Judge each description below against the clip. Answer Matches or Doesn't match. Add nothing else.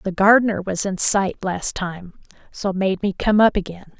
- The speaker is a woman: Matches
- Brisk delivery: Doesn't match